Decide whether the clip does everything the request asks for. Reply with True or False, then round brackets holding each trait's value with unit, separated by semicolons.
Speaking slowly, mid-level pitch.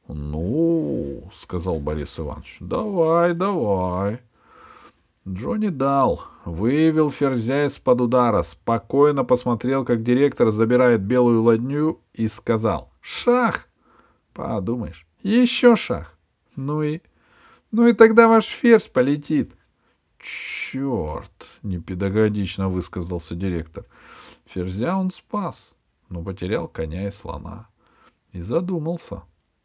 False (95 wpm; 120 Hz)